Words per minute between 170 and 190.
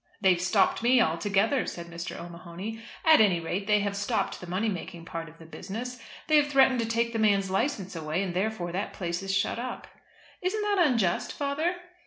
No: average, 200 wpm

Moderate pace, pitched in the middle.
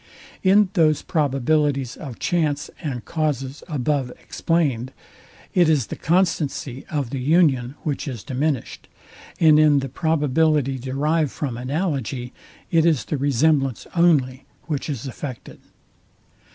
No: slow, 125 wpm; medium, 145 Hz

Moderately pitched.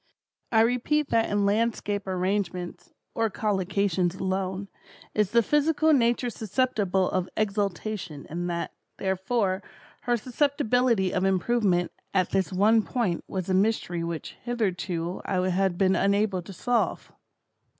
No: high, 200 Hz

